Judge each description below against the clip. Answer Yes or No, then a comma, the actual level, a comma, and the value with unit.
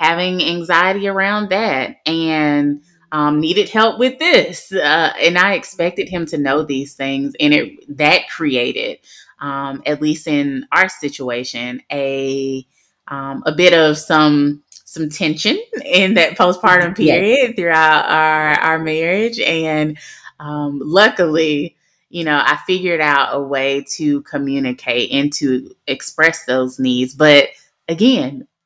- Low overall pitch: No, medium, 155 Hz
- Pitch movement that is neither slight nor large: Yes, average, 4.2 semitones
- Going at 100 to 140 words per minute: Yes, slow, 135 wpm